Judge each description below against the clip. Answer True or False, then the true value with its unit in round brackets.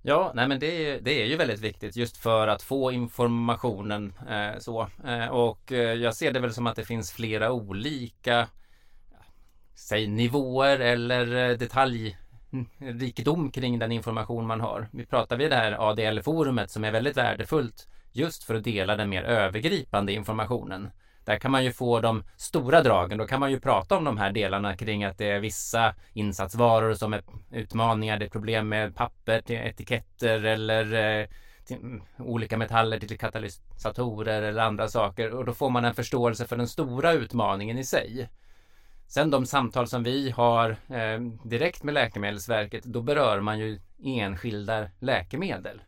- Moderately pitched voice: False (115 Hz)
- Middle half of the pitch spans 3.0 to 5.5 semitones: False (2.4 semitones)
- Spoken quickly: False (160 wpm)